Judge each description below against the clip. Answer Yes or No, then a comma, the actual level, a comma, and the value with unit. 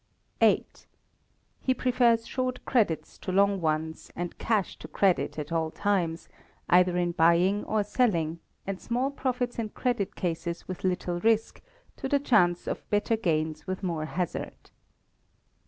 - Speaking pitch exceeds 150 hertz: Yes, medium, 185 Hz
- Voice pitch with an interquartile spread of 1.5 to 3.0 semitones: No, average, 5.1 semitones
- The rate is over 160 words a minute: No, average, 145 wpm